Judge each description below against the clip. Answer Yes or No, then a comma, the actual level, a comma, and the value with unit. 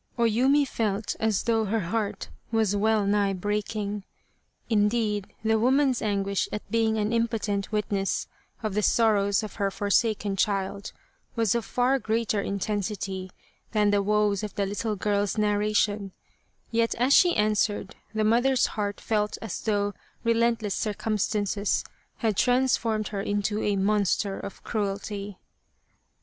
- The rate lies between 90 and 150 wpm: Yes, average, 140 wpm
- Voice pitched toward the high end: Yes, high, 210 Hz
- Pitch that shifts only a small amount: Yes, narrow, 1.8 semitones